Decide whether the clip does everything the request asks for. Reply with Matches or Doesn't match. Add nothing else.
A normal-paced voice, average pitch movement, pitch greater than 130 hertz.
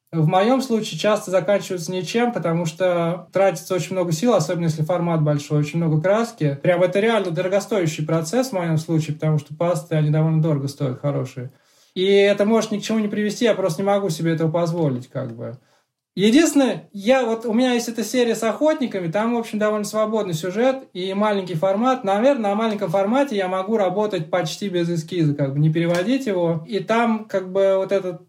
Doesn't match